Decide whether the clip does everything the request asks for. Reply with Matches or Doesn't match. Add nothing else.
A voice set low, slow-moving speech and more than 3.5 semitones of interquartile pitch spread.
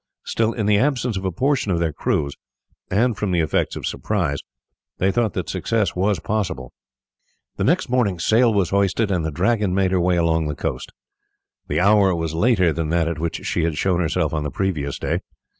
Doesn't match